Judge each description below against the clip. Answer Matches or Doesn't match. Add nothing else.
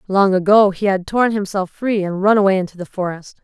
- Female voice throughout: Matches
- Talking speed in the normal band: Doesn't match